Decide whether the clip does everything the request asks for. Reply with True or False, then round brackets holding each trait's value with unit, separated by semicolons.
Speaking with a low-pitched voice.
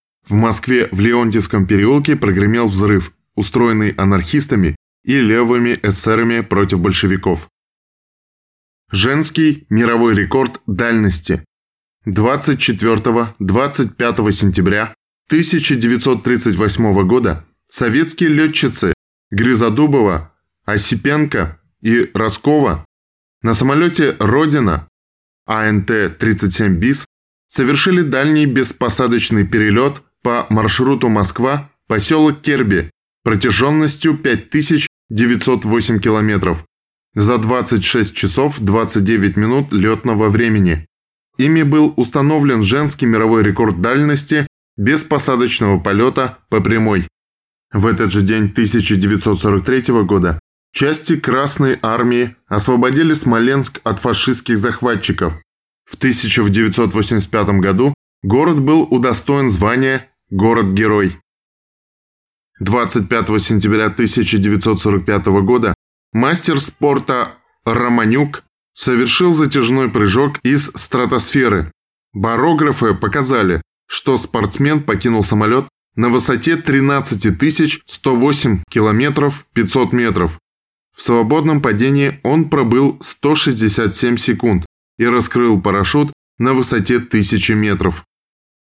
True (115 Hz)